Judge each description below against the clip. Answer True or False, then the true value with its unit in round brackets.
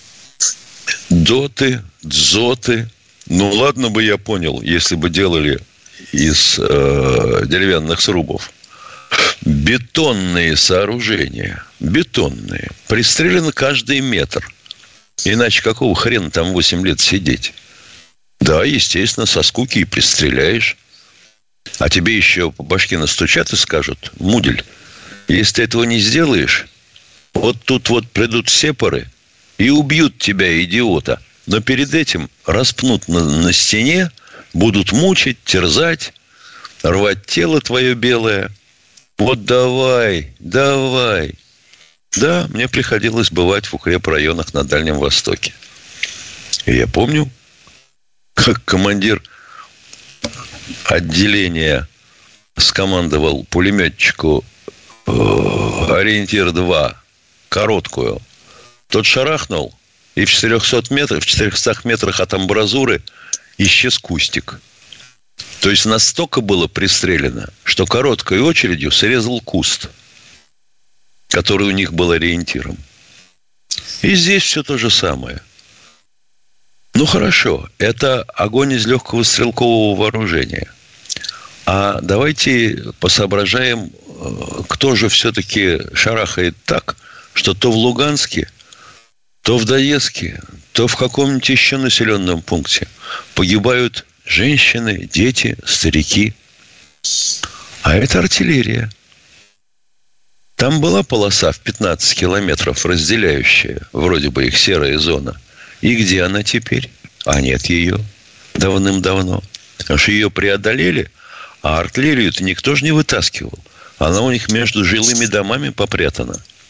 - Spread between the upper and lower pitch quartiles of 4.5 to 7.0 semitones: True (5.6 semitones)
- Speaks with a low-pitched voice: True (105 Hz)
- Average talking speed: False (100 wpm)